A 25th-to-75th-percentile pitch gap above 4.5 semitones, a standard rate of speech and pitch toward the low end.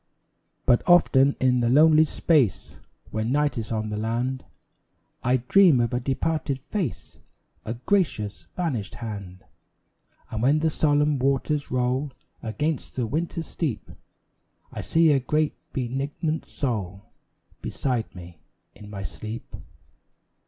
No: average, 5.1 semitones; slow, 125 wpm; low, 130 Hz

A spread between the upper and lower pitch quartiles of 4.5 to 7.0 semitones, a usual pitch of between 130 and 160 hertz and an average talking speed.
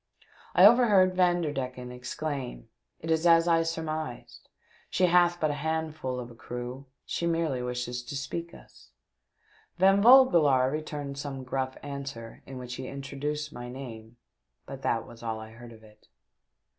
Yes: average, 4.9 semitones; medium, 140 Hz; average, 155 wpm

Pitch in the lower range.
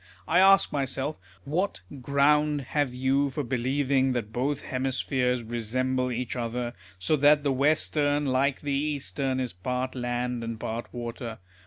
Yes: low, 130 Hz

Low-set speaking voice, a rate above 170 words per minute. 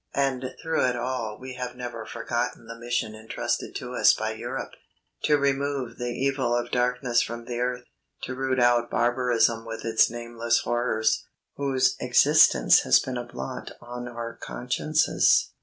No: low, 120 Hz; average, 155 wpm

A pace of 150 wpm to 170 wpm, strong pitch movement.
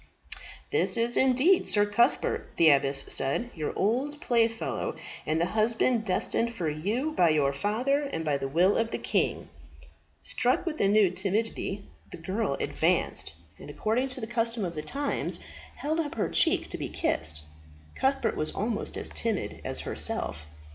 Yes: average, 165 wpm; wide, 6.6 semitones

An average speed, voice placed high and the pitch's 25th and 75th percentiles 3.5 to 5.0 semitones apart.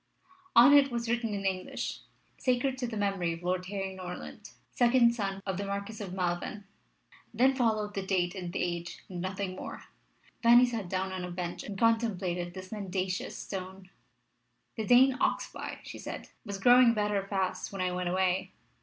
Yes: average, 175 wpm; high, 195 Hz; average, 3.8 semitones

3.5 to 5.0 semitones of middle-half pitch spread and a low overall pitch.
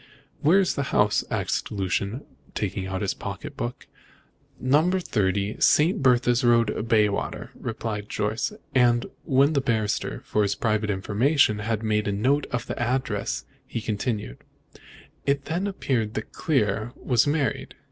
Yes: average, 4.6 semitones; low, 115 Hz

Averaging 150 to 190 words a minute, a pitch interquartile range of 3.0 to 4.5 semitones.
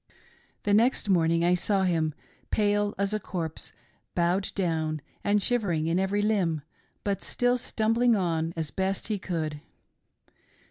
No: average, 140 wpm; average, 3.9 semitones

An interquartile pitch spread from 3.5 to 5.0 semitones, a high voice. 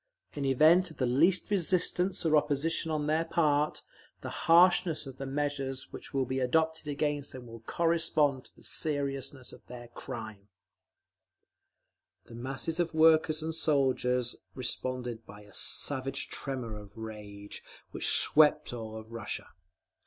No: average, 4.3 semitones; medium, 140 Hz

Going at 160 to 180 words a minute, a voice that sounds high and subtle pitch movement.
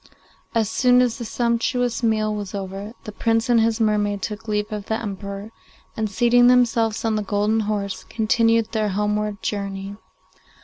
Yes: average, 165 wpm; high, 215 Hz; narrow, 1.9 semitones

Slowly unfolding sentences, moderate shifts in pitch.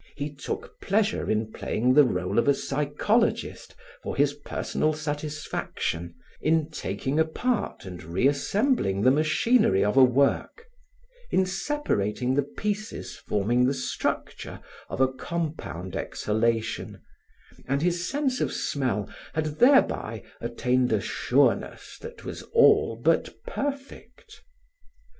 No: slow, 120 wpm; wide, 8.0 semitones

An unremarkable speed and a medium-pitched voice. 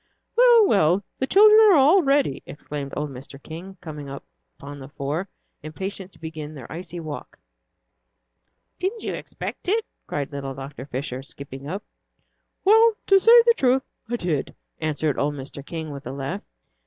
Yes: average, 160 wpm; medium, 155 Hz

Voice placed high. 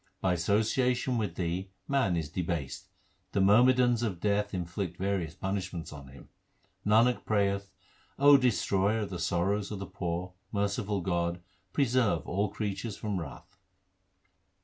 No: low, 100 Hz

